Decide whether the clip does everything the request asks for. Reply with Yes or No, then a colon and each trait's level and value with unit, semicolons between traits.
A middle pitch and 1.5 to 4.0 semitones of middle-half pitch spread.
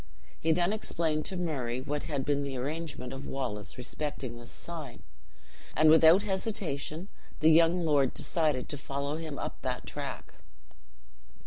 Yes: medium, 150 Hz; average, 3.3 semitones